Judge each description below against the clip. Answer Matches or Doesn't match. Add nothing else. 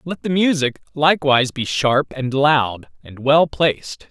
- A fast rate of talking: Doesn't match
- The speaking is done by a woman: Doesn't match